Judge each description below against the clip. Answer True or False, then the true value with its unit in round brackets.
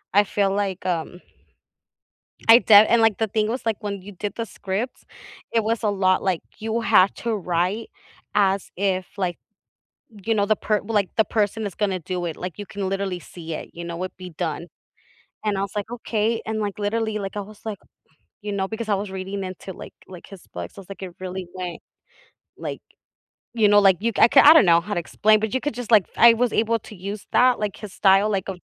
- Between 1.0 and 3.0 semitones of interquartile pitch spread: True (2.6 semitones)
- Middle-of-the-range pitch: False (200 Hz)